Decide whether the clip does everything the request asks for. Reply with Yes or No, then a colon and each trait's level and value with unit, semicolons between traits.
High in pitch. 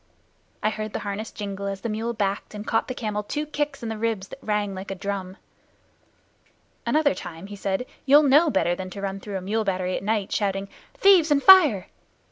Yes: high, 210 Hz